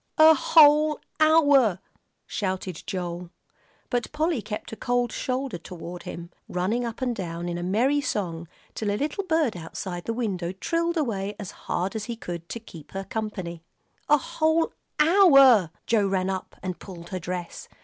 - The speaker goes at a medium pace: Yes, average, 170 wpm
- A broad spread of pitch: Yes, wide, 7.5 semitones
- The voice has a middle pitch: No, high, 210 Hz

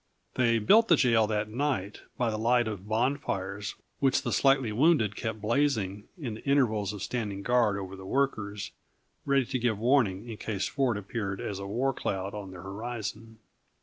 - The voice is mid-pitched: No, low, 110 Hz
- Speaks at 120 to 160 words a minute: No, average, 180 wpm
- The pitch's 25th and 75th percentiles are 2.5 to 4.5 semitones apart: Yes, average, 3.8 semitones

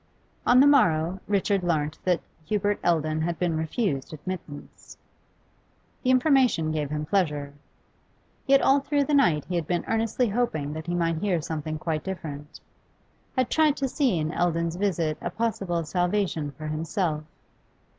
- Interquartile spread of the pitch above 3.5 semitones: Yes, average, 5.1 semitones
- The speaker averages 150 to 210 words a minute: Yes, average, 155 wpm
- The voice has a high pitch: No, medium, 175 Hz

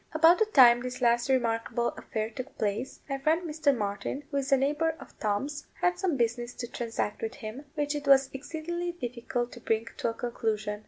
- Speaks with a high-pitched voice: Yes, very high, 255 Hz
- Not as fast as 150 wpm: No, average, 200 wpm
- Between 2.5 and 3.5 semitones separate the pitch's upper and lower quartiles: No, average, 4.1 semitones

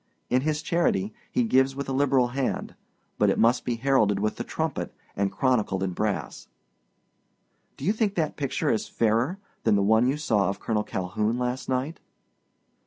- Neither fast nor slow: Yes, average, 175 wpm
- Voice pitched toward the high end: No, low, 125 Hz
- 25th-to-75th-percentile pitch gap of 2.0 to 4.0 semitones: No, average, 4.7 semitones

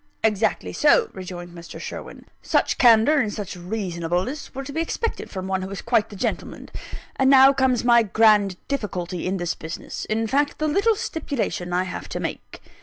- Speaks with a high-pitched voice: Yes, high, 215 Hz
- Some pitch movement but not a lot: No, wide, 6.7 semitones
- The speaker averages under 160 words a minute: No, average, 180 wpm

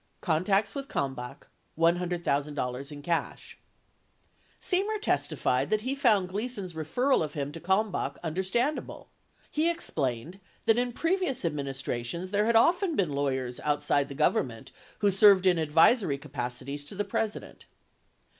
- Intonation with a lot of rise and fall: Yes, wide, 7.6 semitones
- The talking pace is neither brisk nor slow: No, slow, 130 wpm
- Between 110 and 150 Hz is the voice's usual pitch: No, medium, 175 Hz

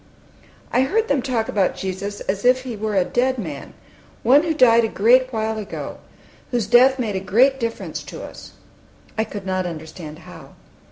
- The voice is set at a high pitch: Yes, high, 225 Hz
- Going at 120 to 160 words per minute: No, average, 180 wpm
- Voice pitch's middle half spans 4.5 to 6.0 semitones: Yes, average, 4.8 semitones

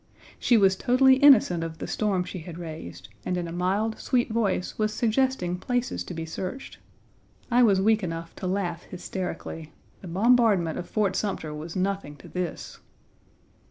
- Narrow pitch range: No, average, 4.5 semitones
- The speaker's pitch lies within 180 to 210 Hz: Yes, high, 190 Hz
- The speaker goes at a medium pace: Yes, average, 165 wpm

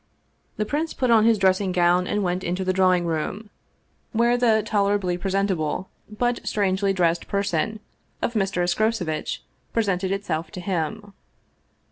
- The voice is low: No, high, 195 Hz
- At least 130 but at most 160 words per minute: Yes, average, 140 wpm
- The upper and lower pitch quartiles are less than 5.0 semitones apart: Yes, average, 3.2 semitones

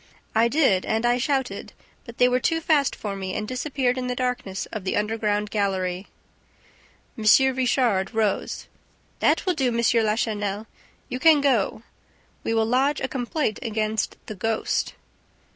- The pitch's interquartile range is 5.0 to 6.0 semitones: No, average, 3.4 semitones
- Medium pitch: No, high, 230 Hz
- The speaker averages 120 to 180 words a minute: Yes, average, 155 wpm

